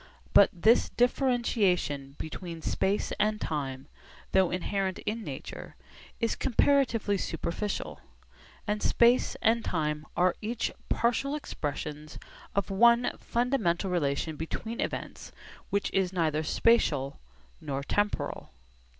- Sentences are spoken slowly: Yes, slow, 105 wpm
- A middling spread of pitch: No, wide, 6.5 semitones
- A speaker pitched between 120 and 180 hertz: No, high, 195 Hz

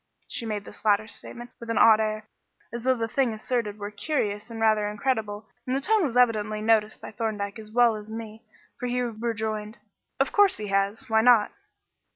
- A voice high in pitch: Yes, high, 220 Hz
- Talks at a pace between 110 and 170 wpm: No, average, 195 wpm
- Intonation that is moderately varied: No, narrow, 2.2 semitones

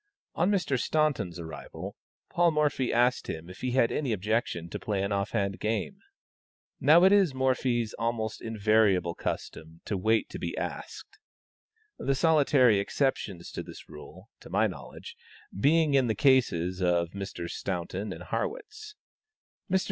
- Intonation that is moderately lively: No, wide, 6.9 semitones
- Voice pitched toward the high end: No, low, 115 Hz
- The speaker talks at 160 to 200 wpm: No, average, 150 wpm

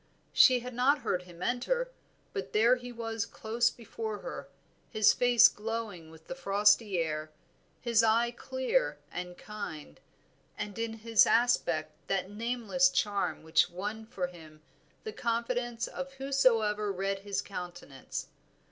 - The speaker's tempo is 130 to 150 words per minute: Yes, average, 140 wpm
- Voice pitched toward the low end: No, high, 220 Hz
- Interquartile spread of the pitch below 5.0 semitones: Yes, average, 4.1 semitones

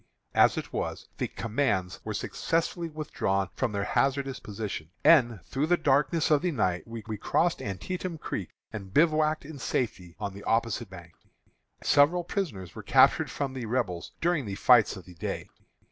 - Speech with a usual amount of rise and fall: No, wide, 7.7 semitones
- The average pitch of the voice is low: Yes, low, 125 Hz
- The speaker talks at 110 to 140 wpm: No, average, 165 wpm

